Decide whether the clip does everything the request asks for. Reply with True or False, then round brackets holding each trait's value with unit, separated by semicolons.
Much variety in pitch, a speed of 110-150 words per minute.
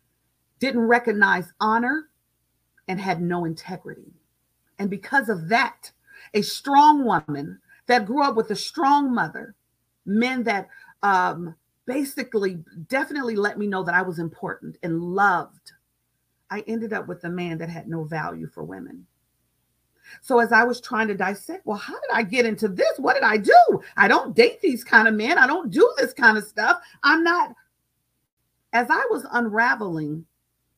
False (6.6 semitones; 165 wpm)